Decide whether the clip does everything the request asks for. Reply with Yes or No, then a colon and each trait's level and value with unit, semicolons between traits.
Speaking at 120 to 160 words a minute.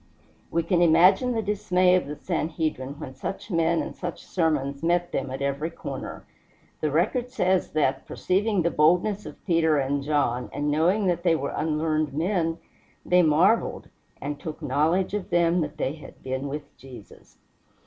No: average, 170 wpm